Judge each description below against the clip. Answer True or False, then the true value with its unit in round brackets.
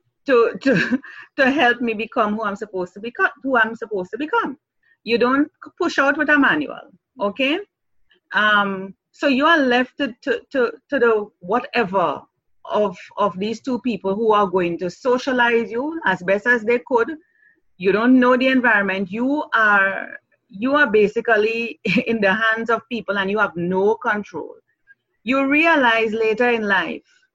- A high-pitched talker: True (235 Hz)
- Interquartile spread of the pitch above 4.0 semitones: True (4.9 semitones)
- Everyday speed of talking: True (165 wpm)